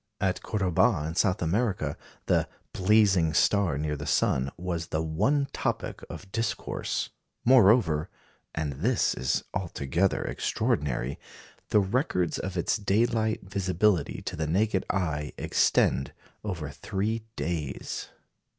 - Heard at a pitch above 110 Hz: No, very low, 90 Hz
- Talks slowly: Yes, slow, 120 wpm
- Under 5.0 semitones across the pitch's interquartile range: No, average, 5.3 semitones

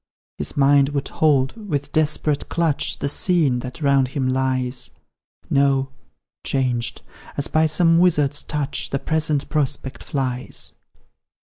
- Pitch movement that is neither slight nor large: No, narrow, 2.3 semitones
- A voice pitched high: No, medium, 140 Hz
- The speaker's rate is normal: No, slow, 125 wpm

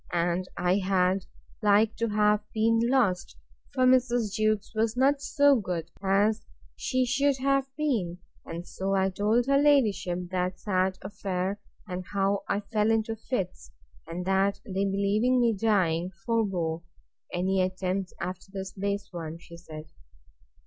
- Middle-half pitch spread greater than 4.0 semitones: No, average, 3.6 semitones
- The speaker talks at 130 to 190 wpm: Yes, average, 140 wpm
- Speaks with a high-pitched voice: Yes, high, 200 Hz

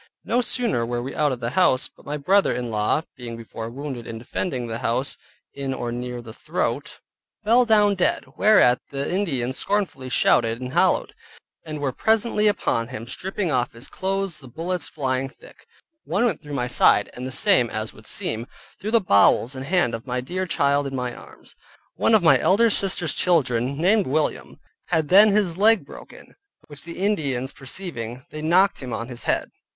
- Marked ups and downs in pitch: Yes, wide, 7.3 semitones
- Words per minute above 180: Yes, average, 190 wpm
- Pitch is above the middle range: No, medium, 140 Hz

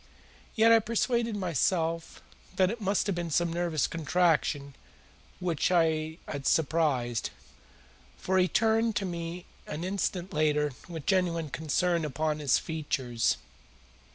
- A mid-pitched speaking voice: Yes, medium, 170 Hz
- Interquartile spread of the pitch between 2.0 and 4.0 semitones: Yes, average, 3.4 semitones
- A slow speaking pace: Yes, slow, 125 wpm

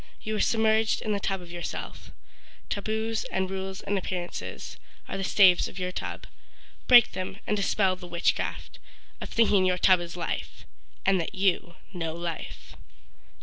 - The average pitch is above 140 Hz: Yes, high, 190 Hz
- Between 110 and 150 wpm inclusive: No, average, 160 wpm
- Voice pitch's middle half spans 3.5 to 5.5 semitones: No, average, 2.7 semitones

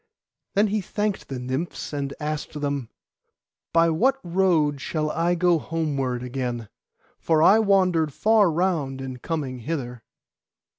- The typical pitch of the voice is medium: Yes, medium, 155 Hz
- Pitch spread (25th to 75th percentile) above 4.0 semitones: Yes, average, 4.8 semitones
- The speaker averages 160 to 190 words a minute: No, slow, 135 wpm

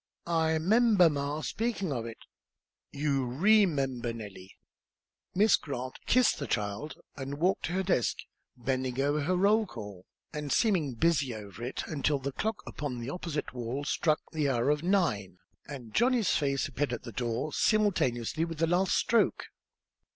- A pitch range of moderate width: No, wide, 6.2 semitones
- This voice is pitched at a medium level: Yes, medium, 145 Hz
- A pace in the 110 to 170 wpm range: Yes, average, 160 wpm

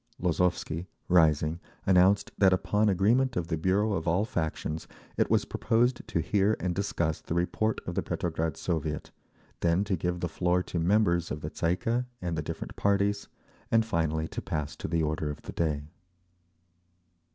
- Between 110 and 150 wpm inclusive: No, average, 175 wpm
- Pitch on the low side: Yes, very low, 90 Hz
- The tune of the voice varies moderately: Yes, average, 3.8 semitones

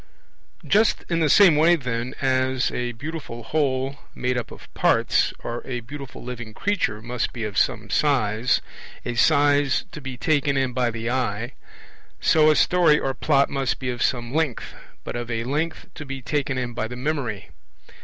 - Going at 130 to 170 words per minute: No, average, 180 wpm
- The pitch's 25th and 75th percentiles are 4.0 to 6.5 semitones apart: No, average, 3.5 semitones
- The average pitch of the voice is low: Yes, low, 130 Hz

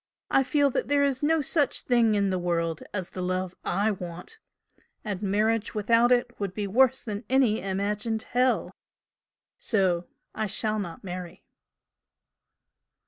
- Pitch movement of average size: Yes, average, 4.7 semitones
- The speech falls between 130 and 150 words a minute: Yes, average, 145 wpm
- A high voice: Yes, high, 210 Hz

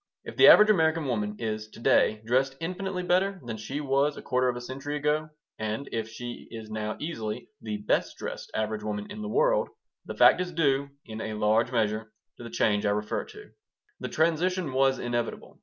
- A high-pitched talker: No, low, 125 Hz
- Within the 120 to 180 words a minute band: No, average, 200 wpm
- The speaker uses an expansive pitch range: Yes, wide, 6.6 semitones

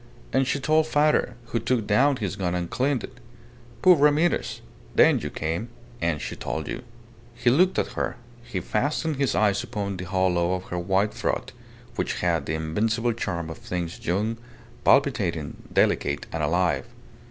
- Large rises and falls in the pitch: Yes, wide, 6.6 semitones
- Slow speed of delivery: No, average, 165 wpm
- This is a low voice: Yes, low, 105 Hz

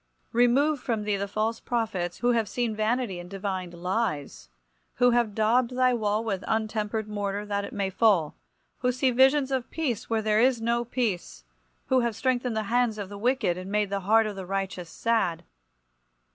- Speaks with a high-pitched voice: Yes, high, 220 Hz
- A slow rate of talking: No, average, 185 wpm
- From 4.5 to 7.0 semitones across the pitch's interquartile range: No, average, 3.4 semitones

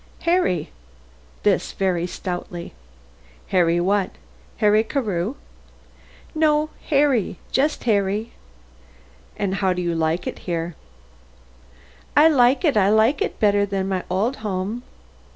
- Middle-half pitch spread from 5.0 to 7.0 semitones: Yes, average, 5.3 semitones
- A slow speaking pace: Yes, slow, 115 wpm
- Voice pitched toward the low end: No, high, 200 Hz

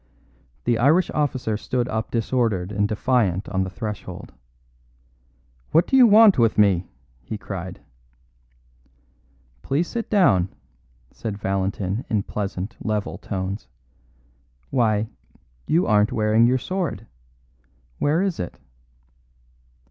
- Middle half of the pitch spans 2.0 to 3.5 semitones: No, average, 5.0 semitones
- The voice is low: Yes, low, 110 Hz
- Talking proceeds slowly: Yes, slow, 110 wpm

